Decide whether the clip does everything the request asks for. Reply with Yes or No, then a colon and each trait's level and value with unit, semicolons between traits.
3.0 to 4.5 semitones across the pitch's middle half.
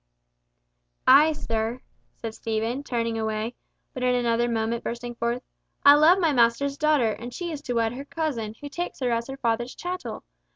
Yes: average, 3.7 semitones